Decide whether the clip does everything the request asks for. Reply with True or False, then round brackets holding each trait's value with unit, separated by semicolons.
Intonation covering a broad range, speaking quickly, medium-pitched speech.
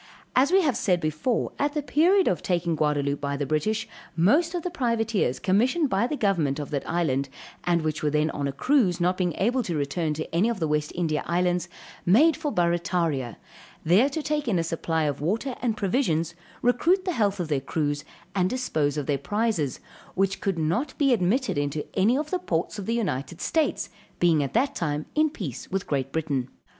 True (8.1 semitones; 215 wpm; 180 Hz)